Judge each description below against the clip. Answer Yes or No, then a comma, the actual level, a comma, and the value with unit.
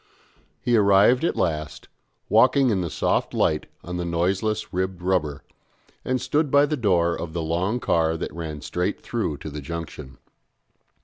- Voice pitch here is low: Yes, very low, 90 Hz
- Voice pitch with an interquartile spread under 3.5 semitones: No, average, 5.0 semitones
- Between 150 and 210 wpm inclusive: Yes, average, 165 wpm